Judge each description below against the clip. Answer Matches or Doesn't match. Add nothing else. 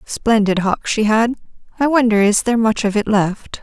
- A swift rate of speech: Doesn't match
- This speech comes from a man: Doesn't match